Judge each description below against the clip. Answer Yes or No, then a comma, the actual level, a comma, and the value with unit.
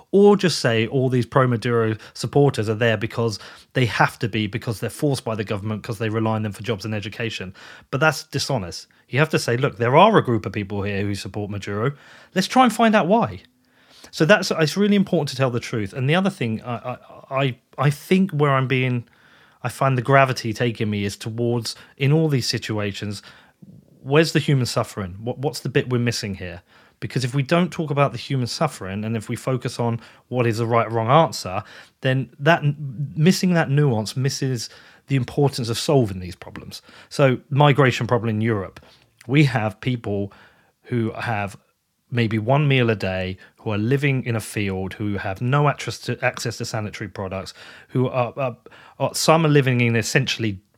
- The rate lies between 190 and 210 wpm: Yes, average, 200 wpm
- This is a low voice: Yes, low, 120 Hz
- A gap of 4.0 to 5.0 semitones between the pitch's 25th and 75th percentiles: Yes, average, 4.3 semitones